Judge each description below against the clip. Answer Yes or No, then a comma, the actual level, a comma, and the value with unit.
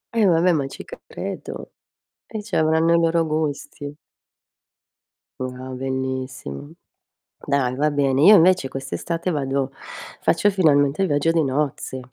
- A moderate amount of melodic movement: Yes, average, 3.7 semitones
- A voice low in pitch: No, medium, 145 Hz